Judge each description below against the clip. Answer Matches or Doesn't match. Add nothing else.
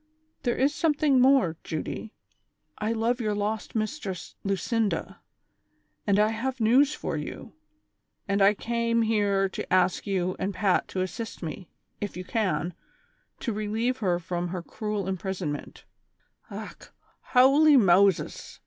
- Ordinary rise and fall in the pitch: Matches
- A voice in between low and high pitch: Doesn't match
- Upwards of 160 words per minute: Doesn't match